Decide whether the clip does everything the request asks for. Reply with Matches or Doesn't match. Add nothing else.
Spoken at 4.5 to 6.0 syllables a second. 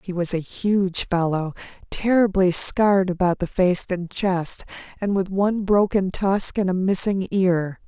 Doesn't match